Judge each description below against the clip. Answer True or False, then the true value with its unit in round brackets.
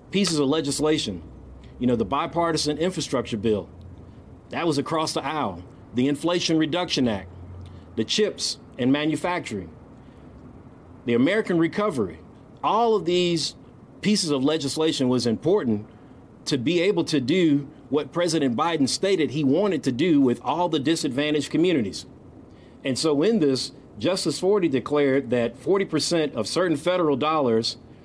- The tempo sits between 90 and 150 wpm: True (135 wpm)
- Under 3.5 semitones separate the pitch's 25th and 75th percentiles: False (5.6 semitones)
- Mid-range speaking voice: True (145 Hz)